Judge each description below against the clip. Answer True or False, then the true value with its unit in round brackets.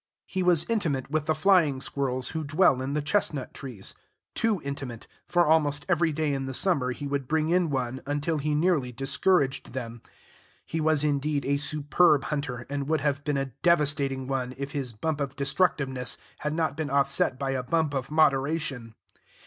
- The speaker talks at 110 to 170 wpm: False (180 wpm)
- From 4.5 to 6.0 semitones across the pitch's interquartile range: False (2.8 semitones)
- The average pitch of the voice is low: False (145 Hz)